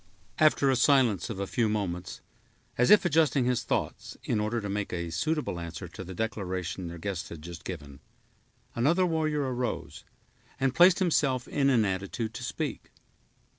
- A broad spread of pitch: Yes, wide, 7.0 semitones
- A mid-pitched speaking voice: No, low, 110 Hz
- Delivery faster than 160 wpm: Yes, average, 170 wpm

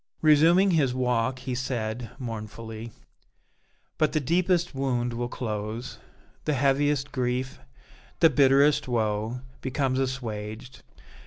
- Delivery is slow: Yes, slow, 105 wpm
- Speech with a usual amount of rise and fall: Yes, average, 3.5 semitones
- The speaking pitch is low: Yes, low, 130 Hz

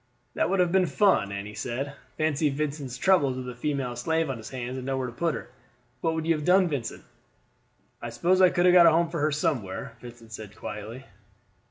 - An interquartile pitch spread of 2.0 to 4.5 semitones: No, wide, 5.4 semitones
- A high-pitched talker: No, medium, 140 Hz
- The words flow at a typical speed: No, fast, 215 wpm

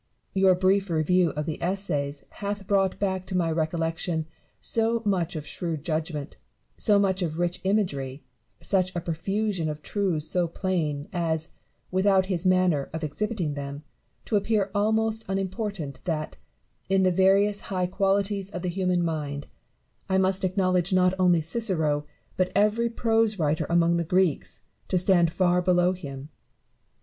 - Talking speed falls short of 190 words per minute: Yes, average, 150 wpm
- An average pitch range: Yes, average, 3.3 semitones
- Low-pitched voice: No, medium, 180 Hz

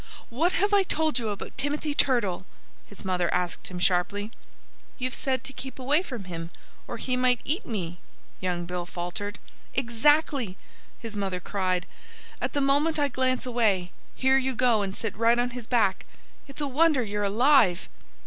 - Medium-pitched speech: No, high, 235 Hz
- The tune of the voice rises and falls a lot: Yes, wide, 6.0 semitones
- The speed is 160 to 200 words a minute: Yes, average, 170 wpm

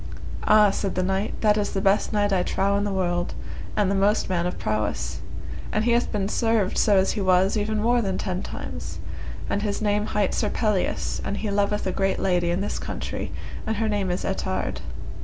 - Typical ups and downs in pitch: No, narrow, 1.9 semitones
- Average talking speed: No, fast, 215 wpm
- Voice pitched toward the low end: No, high, 200 Hz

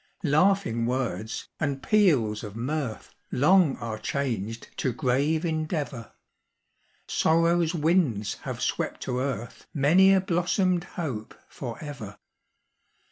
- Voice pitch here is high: No, medium, 140 Hz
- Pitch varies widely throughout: Yes, wide, 6.3 semitones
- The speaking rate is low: Yes, slow, 105 wpm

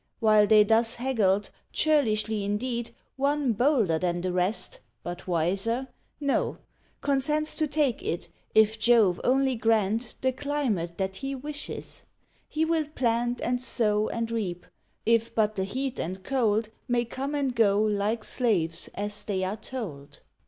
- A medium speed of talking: Yes, average, 145 wpm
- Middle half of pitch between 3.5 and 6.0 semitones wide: Yes, average, 4.5 semitones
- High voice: Yes, high, 225 Hz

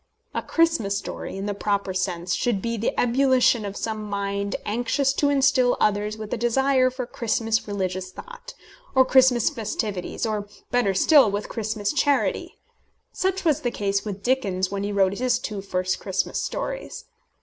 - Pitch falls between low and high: No, high, 220 Hz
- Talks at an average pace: Yes, average, 165 wpm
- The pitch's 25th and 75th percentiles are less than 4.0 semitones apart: No, average, 4.6 semitones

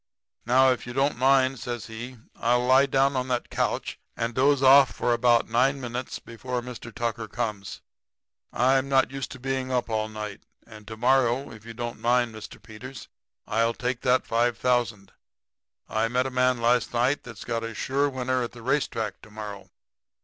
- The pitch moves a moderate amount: No, narrow, 2.2 semitones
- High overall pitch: No, low, 120 Hz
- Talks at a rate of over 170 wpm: Yes, average, 185 wpm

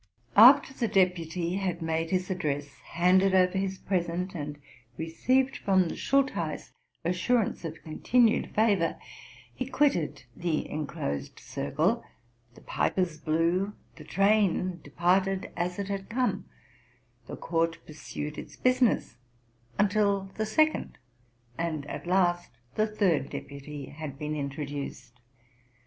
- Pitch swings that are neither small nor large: Yes, average, 4.2 semitones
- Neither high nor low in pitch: Yes, medium, 180 Hz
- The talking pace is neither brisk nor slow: No, slow, 125 wpm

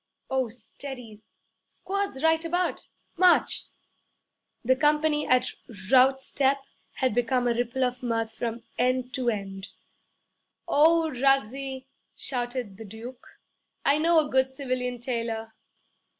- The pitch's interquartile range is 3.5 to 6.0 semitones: No, average, 2.8 semitones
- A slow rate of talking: Yes, slow, 120 wpm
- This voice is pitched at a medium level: No, very high, 255 Hz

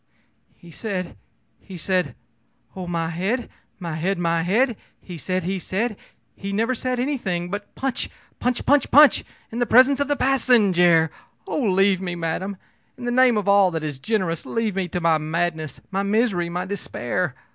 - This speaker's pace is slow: No, average, 170 wpm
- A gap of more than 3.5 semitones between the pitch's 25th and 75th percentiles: Yes, average, 5.1 semitones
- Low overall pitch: No, high, 190 Hz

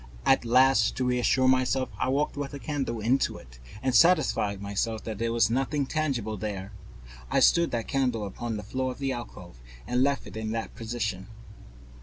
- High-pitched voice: No, low, 120 Hz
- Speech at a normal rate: Yes, average, 180 wpm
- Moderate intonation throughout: Yes, average, 3.6 semitones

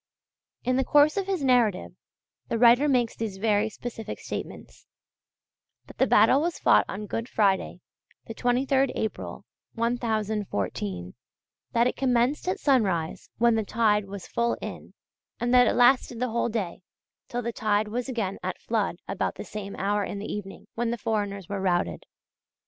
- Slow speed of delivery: No, average, 165 wpm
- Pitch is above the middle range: Yes, high, 225 Hz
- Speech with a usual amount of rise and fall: Yes, average, 3.3 semitones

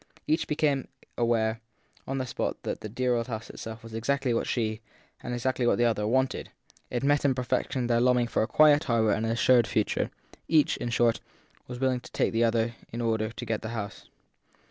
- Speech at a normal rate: No, fast, 210 wpm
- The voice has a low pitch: Yes, low, 120 Hz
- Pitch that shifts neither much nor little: No, narrow, 2.3 semitones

